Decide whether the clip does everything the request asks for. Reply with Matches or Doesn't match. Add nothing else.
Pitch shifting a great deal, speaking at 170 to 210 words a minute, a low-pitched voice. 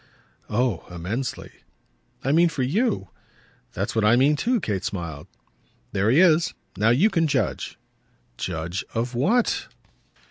Doesn't match